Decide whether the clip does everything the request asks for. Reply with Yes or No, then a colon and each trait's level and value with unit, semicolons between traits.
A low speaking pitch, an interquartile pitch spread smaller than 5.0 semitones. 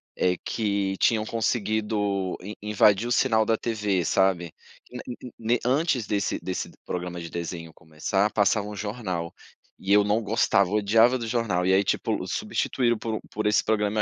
Yes: low, 105 Hz; average, 2.8 semitones